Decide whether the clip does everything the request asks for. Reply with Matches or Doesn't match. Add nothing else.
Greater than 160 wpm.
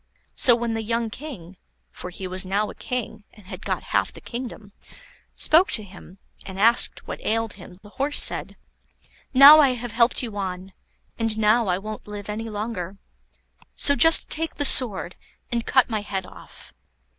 Matches